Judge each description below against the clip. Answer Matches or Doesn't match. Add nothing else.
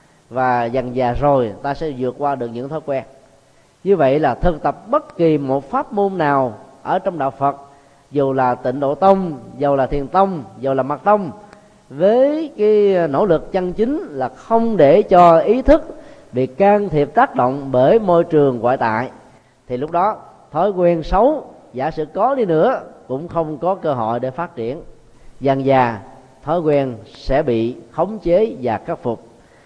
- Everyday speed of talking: Matches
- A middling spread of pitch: Doesn't match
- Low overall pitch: Doesn't match